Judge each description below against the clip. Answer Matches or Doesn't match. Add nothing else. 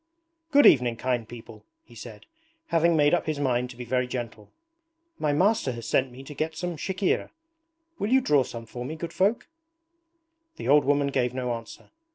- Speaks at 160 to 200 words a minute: Matches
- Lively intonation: Doesn't match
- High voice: Doesn't match